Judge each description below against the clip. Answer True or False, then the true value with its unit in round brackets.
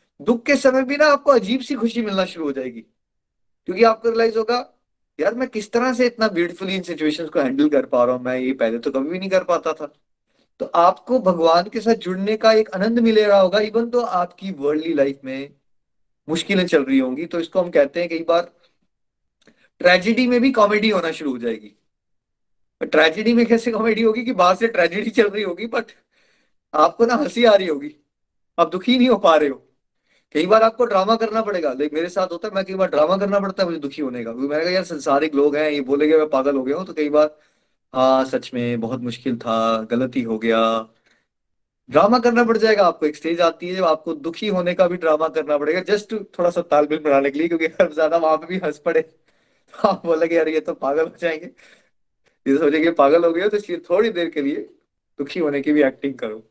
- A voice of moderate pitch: True (170 Hz)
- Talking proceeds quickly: True (225 wpm)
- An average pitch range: False (6.6 semitones)